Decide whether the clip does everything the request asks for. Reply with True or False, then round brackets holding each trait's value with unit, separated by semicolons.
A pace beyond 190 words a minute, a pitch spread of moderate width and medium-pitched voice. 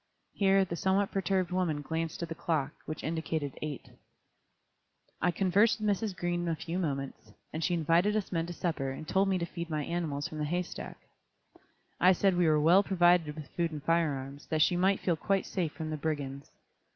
True (205 wpm; 3.1 semitones; 170 Hz)